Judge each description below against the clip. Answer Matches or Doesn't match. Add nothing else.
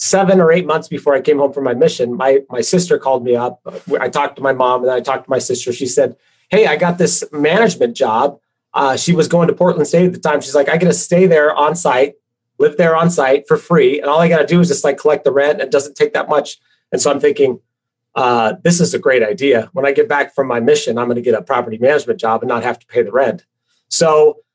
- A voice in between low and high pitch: Matches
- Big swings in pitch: Matches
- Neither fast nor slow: Doesn't match